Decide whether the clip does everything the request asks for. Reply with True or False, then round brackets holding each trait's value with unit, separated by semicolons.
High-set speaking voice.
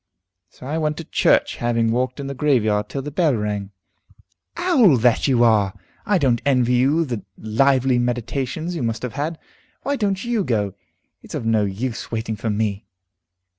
False (125 Hz)